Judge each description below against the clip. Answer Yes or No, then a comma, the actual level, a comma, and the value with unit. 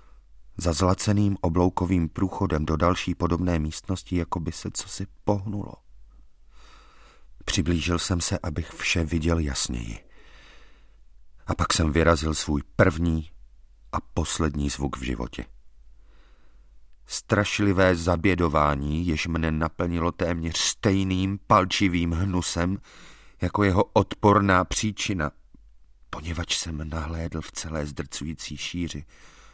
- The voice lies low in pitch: Yes, very low, 85 Hz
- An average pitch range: Yes, average, 3.9 semitones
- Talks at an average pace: No, slow, 105 wpm